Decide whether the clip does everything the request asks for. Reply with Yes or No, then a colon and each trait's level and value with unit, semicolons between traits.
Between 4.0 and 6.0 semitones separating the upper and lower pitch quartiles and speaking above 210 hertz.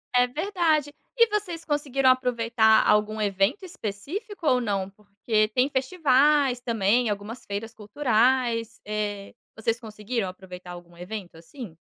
Yes: average, 4.8 semitones; high, 230 Hz